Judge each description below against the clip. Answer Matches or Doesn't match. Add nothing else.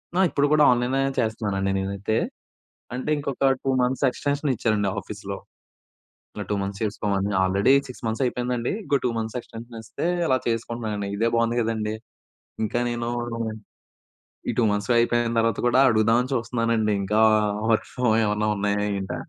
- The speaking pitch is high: Doesn't match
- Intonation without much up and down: Doesn't match